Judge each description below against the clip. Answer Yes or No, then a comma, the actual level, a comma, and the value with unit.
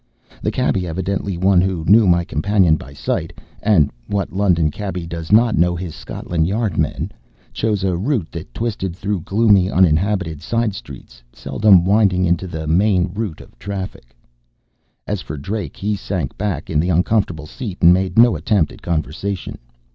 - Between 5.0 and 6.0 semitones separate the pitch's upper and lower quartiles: No, average, 3.5 semitones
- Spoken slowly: No, average, 165 wpm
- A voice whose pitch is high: No, very low, 95 Hz